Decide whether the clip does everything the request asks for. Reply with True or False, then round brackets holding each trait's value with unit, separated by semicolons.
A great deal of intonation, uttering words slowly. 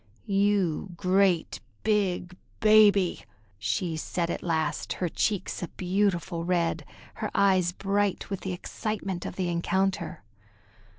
False (2.4 semitones; 120 wpm)